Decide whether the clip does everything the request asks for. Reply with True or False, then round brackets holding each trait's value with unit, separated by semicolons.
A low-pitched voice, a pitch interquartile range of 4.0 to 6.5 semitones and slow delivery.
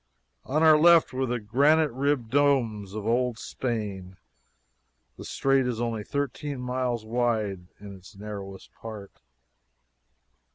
True (120 Hz; 4.5 semitones; 125 wpm)